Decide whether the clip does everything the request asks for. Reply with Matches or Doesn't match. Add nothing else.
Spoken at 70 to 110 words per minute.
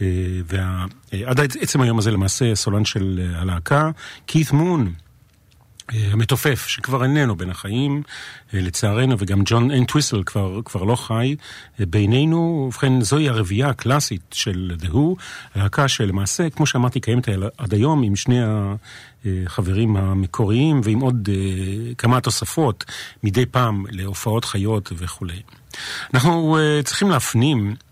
Doesn't match